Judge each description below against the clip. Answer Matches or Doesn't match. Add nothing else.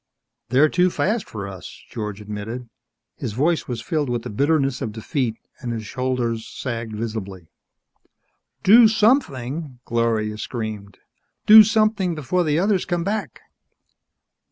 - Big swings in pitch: Matches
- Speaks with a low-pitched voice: Matches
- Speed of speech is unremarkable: Doesn't match